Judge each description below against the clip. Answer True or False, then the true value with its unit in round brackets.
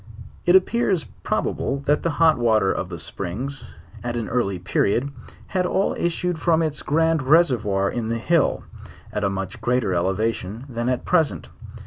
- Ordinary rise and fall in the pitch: False (7.8 semitones)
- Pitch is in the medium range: False (125 Hz)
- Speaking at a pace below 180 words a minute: True (160 wpm)